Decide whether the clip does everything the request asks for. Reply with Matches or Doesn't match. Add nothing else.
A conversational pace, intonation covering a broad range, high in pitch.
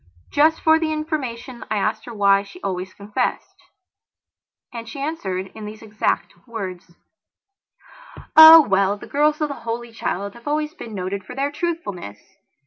Matches